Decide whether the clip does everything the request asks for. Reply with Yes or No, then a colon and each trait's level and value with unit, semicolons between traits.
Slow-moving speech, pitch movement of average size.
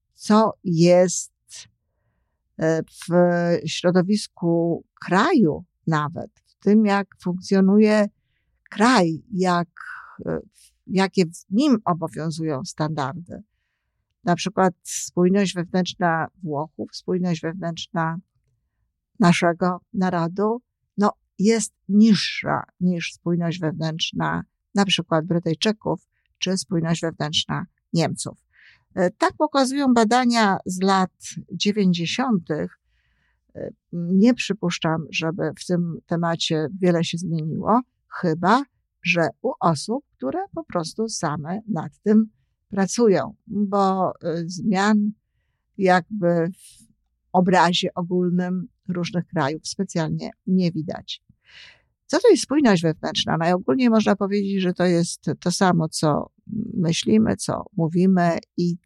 Yes: slow, 95 wpm; average, 3.5 semitones